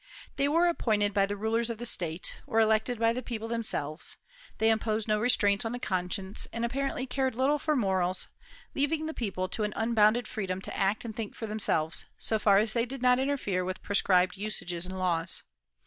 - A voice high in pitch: Yes, high, 220 Hz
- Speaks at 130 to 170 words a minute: No, average, 200 wpm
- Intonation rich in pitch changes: No, average, 3.8 semitones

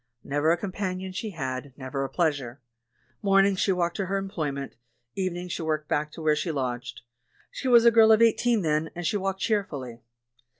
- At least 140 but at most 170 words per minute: No, average, 200 wpm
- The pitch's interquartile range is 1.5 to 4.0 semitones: No, average, 5.1 semitones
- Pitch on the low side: No, medium, 175 Hz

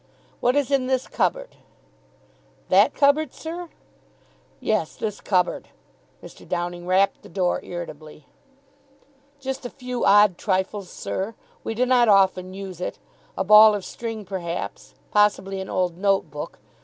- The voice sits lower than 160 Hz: No, high, 200 Hz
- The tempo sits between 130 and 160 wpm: Yes, average, 140 wpm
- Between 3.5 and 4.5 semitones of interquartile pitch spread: No, average, 5.0 semitones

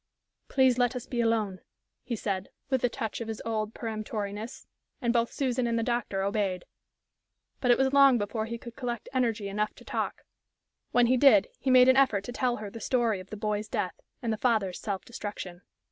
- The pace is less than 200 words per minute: No, fast, 205 wpm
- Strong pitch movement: No, average, 2.9 semitones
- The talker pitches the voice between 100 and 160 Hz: No, high, 230 Hz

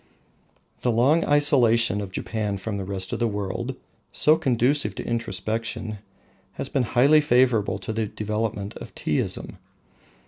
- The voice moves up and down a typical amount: Yes, average, 3.6 semitones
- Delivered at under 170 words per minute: Yes, average, 140 wpm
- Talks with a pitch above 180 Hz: No, low, 115 Hz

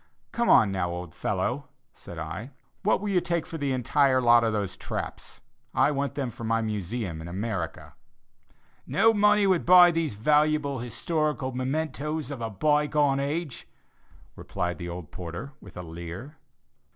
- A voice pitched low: Yes, low, 130 Hz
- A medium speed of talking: Yes, average, 160 wpm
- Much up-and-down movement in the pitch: Yes, wide, 7.5 semitones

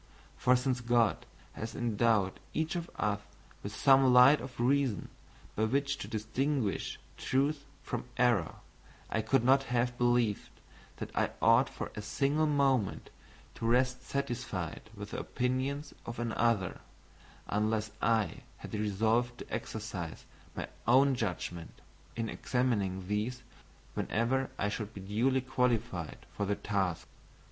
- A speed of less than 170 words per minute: Yes, slow, 135 wpm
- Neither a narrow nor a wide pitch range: Yes, average, 3.7 semitones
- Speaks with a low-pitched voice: Yes, low, 120 Hz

